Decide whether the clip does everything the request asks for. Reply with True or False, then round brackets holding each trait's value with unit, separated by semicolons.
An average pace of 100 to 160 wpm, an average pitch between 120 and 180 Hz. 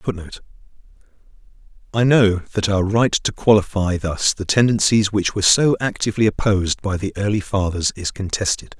False (150 wpm; 100 Hz)